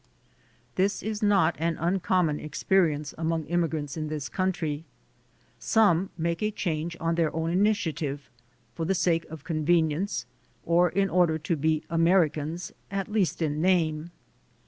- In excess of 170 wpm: No, average, 145 wpm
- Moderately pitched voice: Yes, medium, 165 Hz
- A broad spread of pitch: No, average, 3.0 semitones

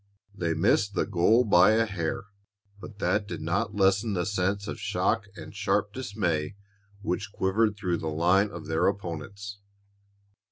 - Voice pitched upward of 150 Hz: No, low, 100 Hz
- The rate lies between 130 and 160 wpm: Yes, average, 155 wpm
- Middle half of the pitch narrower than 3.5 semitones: Yes, average, 2.9 semitones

